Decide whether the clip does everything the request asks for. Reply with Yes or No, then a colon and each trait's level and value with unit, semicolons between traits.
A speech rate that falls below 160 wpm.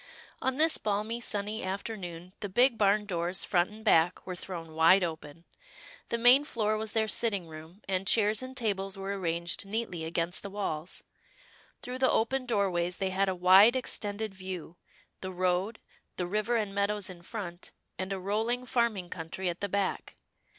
No: average, 180 wpm